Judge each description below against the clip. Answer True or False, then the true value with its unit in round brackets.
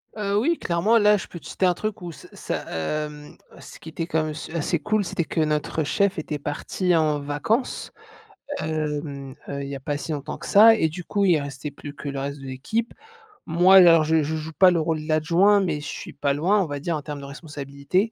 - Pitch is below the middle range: False (155 Hz)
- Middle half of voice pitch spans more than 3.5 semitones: True (4.0 semitones)